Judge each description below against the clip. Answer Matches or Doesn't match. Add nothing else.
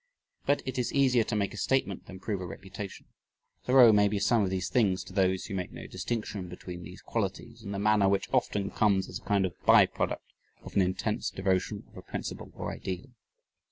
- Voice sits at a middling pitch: Doesn't match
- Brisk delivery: Matches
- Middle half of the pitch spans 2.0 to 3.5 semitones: Matches